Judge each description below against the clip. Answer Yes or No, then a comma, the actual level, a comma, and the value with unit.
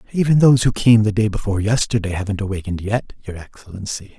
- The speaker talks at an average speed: Yes, average, 185 wpm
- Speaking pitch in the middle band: No, low, 105 Hz